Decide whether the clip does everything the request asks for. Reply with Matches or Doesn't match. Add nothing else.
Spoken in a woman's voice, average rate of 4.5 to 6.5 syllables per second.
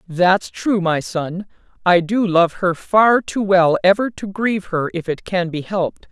Doesn't match